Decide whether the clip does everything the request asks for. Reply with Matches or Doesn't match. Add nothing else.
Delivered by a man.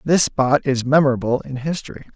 Matches